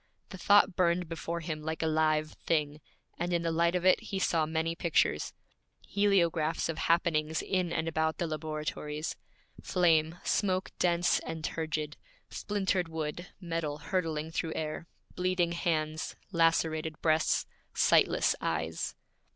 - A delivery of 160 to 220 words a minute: No, slow, 135 wpm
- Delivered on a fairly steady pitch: Yes, narrow, 2.0 semitones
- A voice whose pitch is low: No, medium, 165 Hz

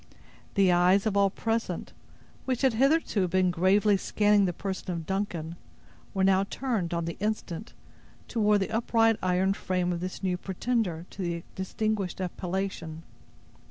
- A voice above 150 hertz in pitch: Yes, high, 190 Hz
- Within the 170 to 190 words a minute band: No, average, 150 wpm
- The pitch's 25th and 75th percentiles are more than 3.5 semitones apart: No, average, 2.9 semitones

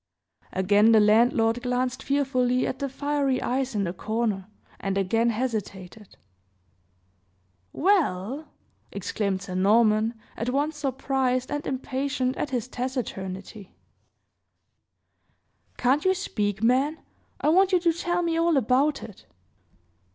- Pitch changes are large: No, average, 4.8 semitones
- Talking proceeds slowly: Yes, slow, 120 wpm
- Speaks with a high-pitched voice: Yes, very high, 250 Hz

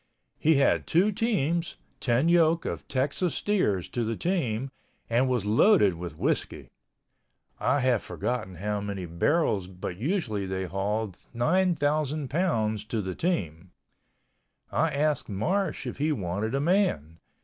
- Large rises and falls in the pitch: Yes, wide, 8.4 semitones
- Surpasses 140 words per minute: No, slow, 135 wpm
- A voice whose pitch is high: No, low, 125 Hz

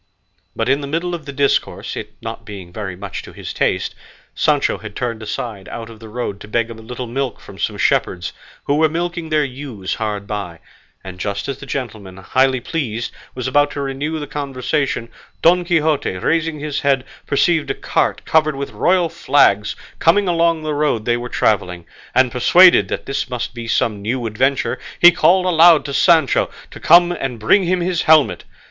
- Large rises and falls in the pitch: Yes, wide, 5.9 semitones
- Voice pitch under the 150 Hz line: Yes, low, 135 Hz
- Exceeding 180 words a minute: Yes, average, 190 wpm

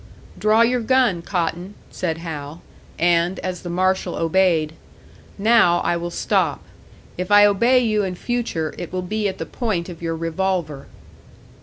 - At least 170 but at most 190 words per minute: No, average, 155 wpm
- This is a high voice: No, medium, 180 Hz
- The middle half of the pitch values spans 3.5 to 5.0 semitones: Yes, average, 3.8 semitones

